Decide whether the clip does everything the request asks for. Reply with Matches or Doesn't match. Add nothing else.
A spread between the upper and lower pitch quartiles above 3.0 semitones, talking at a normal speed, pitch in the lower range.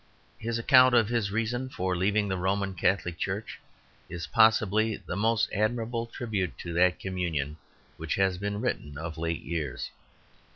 Matches